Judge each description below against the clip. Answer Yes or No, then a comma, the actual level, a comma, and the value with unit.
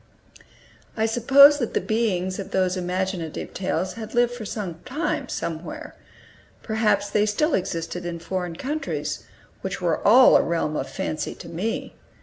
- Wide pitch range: No, average, 5.0 semitones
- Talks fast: No, average, 145 wpm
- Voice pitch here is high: Yes, high, 200 Hz